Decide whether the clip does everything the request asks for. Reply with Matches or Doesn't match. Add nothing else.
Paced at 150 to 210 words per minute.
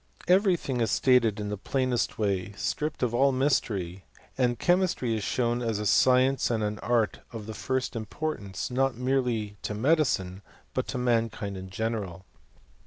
Matches